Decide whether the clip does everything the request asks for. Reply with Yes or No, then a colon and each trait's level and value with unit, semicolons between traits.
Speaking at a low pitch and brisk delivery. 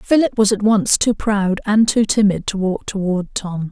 No: high, 205 Hz; fast, 210 wpm